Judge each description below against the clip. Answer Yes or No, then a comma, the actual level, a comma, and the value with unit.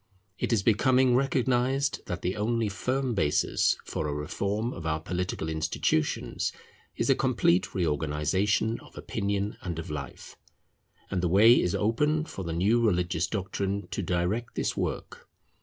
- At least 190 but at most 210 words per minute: No, average, 150 wpm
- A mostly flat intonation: No, wide, 5.4 semitones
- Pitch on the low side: Yes, low, 100 Hz